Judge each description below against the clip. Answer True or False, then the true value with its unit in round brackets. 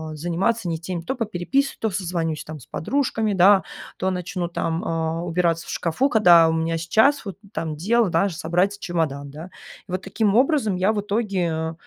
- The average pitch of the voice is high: False (180 Hz)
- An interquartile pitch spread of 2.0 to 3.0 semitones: False (3.9 semitones)